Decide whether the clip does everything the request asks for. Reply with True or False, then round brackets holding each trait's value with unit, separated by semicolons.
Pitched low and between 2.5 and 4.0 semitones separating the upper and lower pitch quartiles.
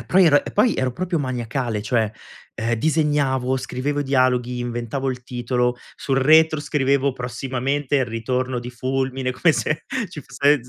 True (130 Hz; 2.8 semitones)